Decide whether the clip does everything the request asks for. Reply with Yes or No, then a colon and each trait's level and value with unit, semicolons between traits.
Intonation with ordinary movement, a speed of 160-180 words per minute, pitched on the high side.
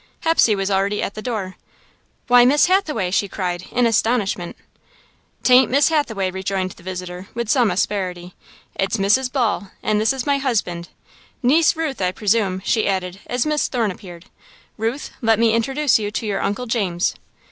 Yes: average, 4.7 semitones; average, 170 wpm; high, 215 Hz